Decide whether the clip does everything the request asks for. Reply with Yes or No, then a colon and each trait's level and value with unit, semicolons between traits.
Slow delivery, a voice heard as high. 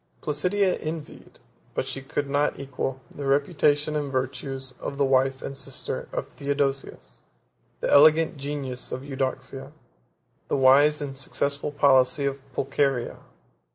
No: slow, 130 wpm; medium, 140 Hz